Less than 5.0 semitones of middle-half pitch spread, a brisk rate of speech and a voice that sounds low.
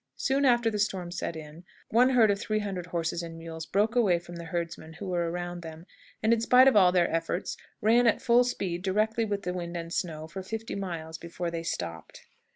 No: average, 4.4 semitones; fast, 220 wpm; medium, 180 Hz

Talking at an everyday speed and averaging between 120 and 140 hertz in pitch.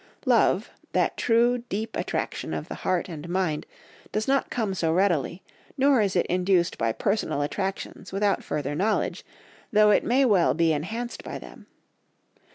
No: average, 160 wpm; high, 195 Hz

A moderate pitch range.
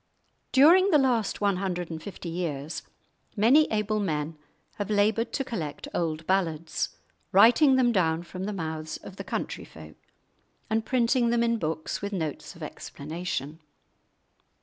No: wide, 6.3 semitones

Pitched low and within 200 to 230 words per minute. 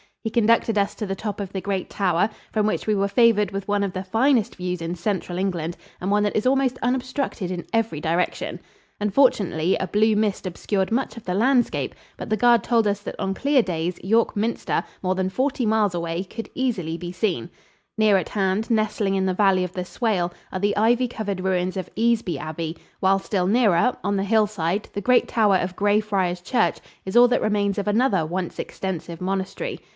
No: high, 200 Hz; fast, 205 wpm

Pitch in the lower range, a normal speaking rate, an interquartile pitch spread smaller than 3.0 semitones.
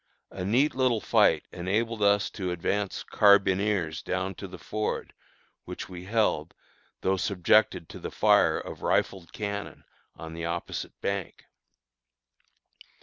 No: low, 100 Hz; slow, 130 wpm; narrow, 2.6 semitones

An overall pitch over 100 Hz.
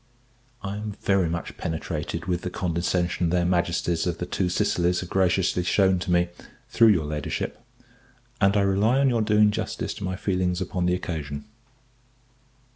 No: very low, 90 Hz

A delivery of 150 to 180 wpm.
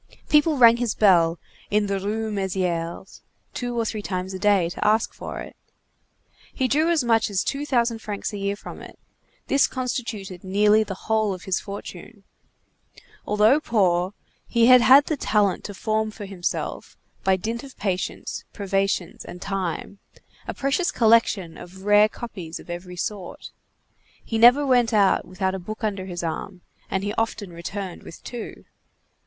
Yes: average, 165 wpm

